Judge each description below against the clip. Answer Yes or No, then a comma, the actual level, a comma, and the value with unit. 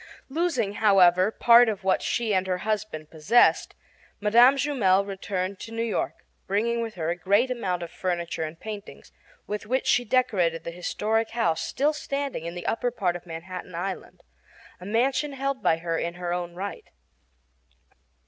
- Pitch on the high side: Yes, high, 200 Hz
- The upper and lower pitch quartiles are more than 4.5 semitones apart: Yes, average, 5.0 semitones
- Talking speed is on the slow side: No, average, 165 wpm